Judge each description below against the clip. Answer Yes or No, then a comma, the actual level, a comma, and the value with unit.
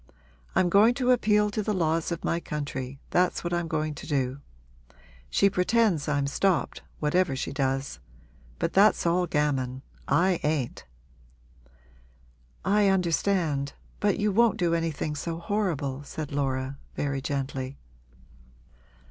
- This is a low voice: No, medium, 165 Hz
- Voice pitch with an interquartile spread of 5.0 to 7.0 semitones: Yes, wide, 5.4 semitones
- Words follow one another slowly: Yes, slow, 130 wpm